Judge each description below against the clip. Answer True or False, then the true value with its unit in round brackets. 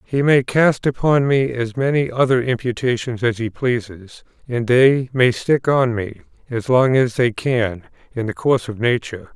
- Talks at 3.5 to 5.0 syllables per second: True (4.5 syllables/s)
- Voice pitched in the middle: False (125 Hz)